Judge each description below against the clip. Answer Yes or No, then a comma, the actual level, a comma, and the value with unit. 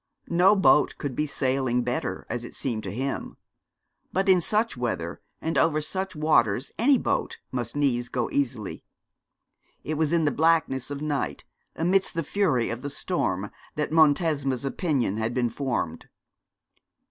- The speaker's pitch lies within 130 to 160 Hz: Yes, medium, 140 Hz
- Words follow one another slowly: No, average, 155 wpm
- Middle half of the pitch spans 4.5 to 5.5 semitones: Yes, average, 5.0 semitones